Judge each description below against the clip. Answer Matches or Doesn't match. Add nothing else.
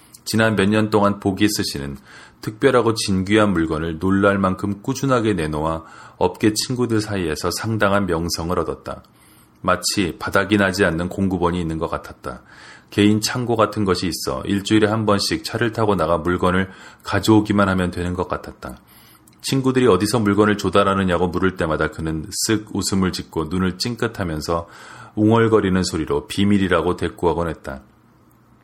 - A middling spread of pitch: Matches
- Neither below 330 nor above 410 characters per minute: Matches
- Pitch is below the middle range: Matches